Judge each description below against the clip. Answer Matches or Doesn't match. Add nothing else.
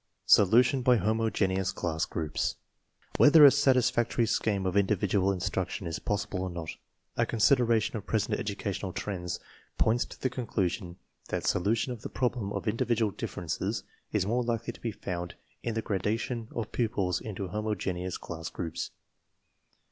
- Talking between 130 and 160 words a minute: Matches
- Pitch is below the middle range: Matches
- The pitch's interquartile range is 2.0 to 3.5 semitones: Doesn't match